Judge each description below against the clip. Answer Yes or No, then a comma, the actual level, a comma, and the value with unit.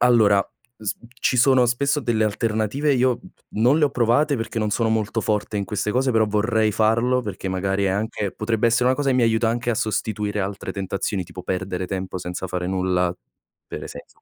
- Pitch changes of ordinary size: Yes, average, 3.6 semitones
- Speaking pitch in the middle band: No, low, 110 Hz